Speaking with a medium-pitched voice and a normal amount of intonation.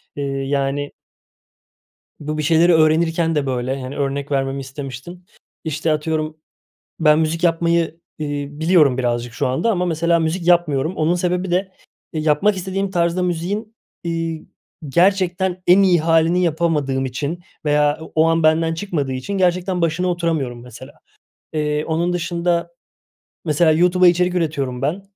Yes: medium, 160 Hz; average, 3.3 semitones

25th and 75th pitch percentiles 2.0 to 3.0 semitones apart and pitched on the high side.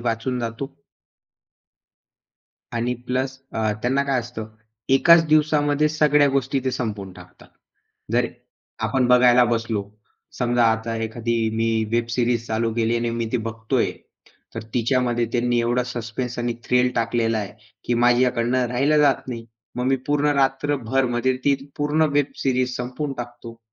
No: narrow, 2.4 semitones; low, 125 Hz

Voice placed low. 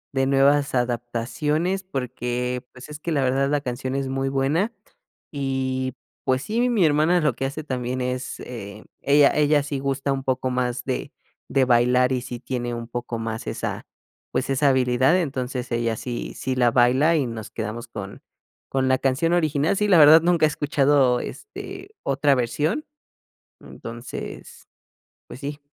Yes: low, 130 Hz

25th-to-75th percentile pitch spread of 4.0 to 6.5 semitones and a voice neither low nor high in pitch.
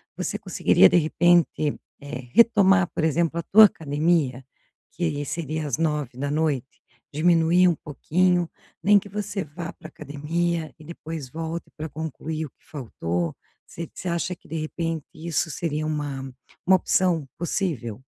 No: average, 2.8 semitones; medium, 160 Hz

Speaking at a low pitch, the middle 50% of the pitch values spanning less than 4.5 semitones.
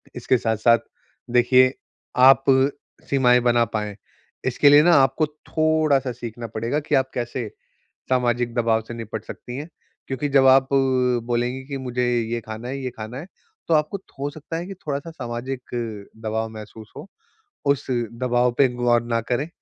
Yes: low, 125 Hz; average, 2.8 semitones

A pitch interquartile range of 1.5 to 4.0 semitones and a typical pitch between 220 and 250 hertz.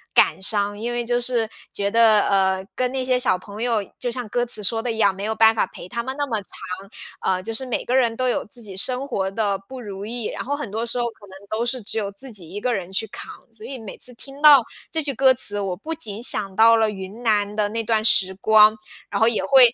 Yes: average, 3.2 semitones; high, 225 Hz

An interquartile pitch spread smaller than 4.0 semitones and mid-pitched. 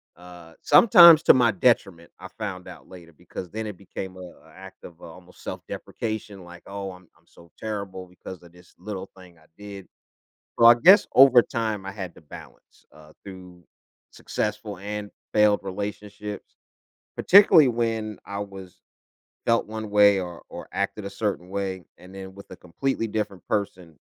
No: average, 2.9 semitones; low, 100 Hz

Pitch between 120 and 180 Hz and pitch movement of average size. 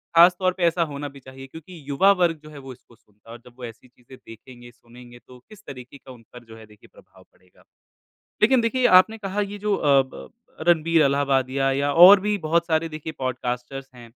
No: medium, 140 Hz; wide, 6.0 semitones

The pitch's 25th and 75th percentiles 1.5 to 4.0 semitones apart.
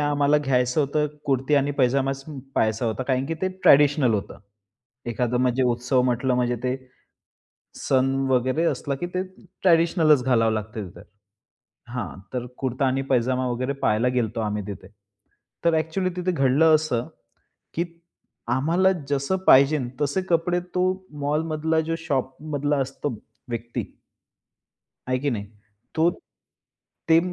Yes: average, 3.7 semitones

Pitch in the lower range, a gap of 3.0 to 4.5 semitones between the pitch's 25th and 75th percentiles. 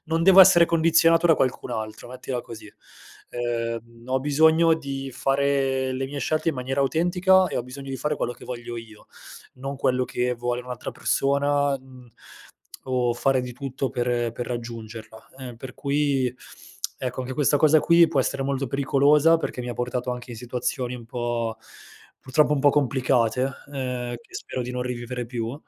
No: low, 130 Hz; narrow, 2.6 semitones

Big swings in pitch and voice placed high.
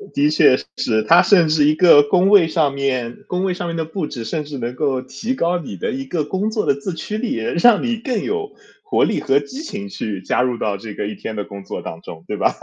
No: wide, 7.3 semitones; medium, 150 Hz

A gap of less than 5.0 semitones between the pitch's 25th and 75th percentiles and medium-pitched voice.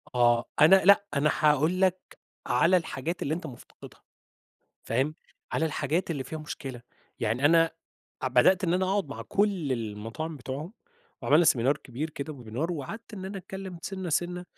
No: wide, 5.5 semitones; medium, 155 Hz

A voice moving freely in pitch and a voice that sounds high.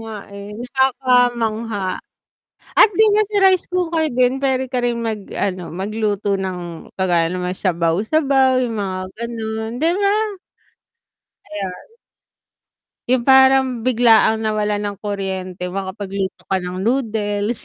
No: average, 4.7 semitones; high, 220 Hz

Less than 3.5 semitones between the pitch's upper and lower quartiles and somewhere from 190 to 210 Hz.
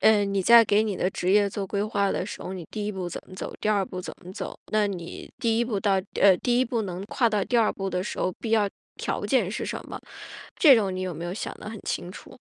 Yes: average, 2.7 semitones; high, 200 Hz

